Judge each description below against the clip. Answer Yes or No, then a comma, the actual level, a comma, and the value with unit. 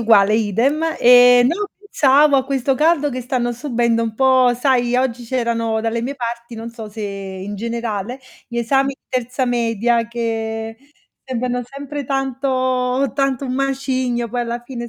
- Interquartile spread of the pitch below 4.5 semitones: Yes, narrow, 2.4 semitones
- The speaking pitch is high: Yes, high, 245 Hz